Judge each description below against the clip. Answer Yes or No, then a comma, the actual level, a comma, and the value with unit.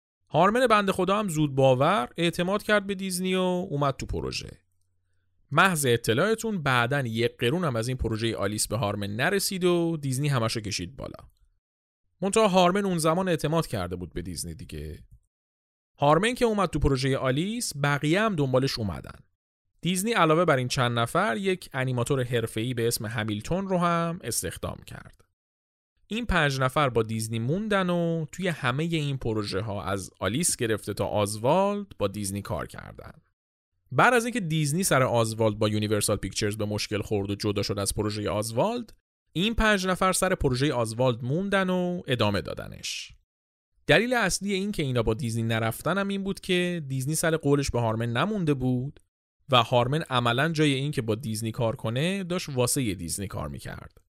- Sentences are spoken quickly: Yes, fast, 165 wpm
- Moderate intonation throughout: No, wide, 8.7 semitones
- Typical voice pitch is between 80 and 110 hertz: No, low, 130 Hz